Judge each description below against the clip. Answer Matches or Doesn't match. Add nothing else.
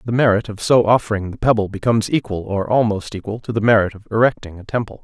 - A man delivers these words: Matches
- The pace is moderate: Doesn't match